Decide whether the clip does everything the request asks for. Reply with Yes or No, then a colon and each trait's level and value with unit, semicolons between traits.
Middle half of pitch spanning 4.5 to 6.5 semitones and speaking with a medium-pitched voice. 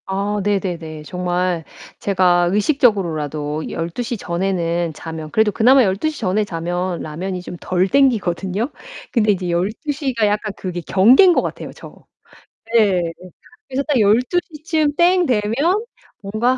No: wide, 5.5 semitones; high, 195 Hz